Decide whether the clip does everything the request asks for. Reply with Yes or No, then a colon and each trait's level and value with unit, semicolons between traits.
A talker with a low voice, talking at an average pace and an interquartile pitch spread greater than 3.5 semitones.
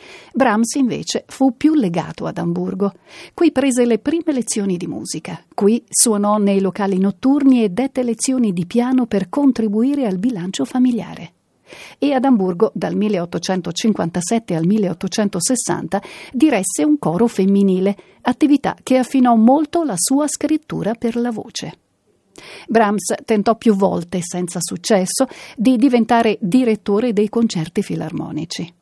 No: high, 220 Hz; average, 130 wpm; average, 5.0 semitones